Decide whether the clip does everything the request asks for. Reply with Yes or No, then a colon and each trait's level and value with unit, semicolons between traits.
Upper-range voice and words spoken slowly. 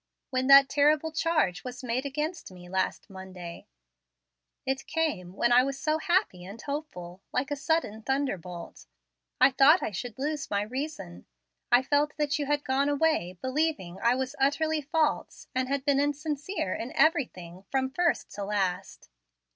No: very high, 270 Hz; average, 160 wpm